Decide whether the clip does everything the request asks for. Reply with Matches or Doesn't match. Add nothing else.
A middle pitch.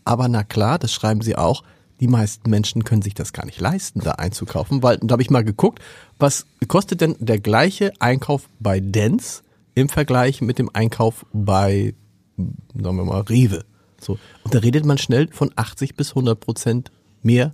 Doesn't match